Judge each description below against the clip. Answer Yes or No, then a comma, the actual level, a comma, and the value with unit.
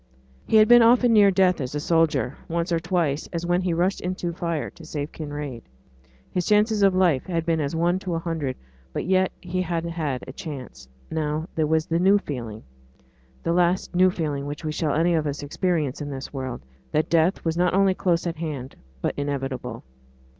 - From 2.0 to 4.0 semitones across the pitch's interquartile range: Yes, average, 3.7 semitones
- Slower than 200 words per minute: No, fast, 205 wpm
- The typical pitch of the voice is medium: Yes, medium, 165 Hz